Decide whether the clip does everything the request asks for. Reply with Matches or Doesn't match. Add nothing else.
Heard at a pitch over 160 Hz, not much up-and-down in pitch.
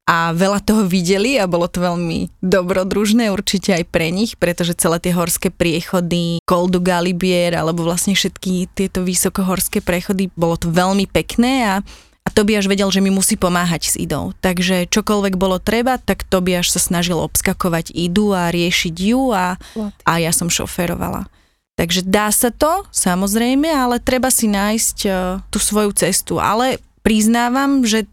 Doesn't match